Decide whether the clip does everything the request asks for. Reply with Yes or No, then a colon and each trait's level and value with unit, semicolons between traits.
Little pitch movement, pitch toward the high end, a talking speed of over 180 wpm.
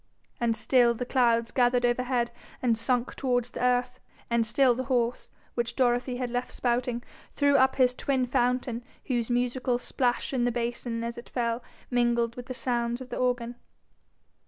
No: narrow, 1.0 semitones; high, 245 Hz; average, 170 wpm